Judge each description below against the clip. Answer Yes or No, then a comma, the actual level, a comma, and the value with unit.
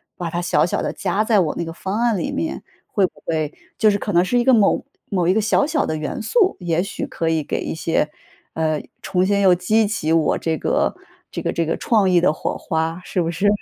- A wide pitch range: No, average, 4.2 semitones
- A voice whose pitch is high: No, medium, 180 Hz